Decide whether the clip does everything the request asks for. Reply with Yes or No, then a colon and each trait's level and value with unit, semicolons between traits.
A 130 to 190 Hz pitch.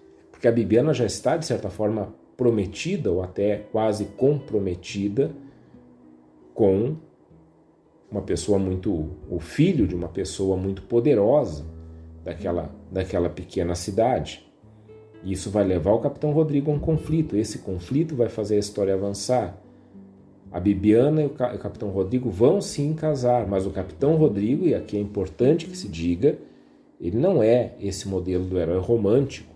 No: low, 105 Hz